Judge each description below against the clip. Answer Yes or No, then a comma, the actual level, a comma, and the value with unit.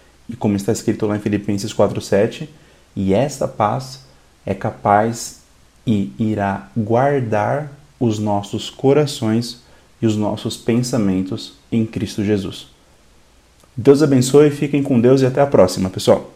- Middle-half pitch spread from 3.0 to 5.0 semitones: Yes, average, 4.0 semitones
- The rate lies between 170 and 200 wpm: No, average, 130 wpm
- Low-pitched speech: Yes, low, 115 Hz